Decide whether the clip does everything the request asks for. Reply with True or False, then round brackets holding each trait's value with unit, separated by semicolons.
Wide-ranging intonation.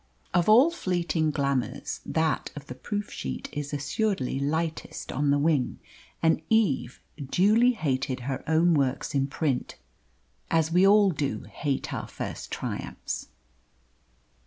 False (4.7 semitones)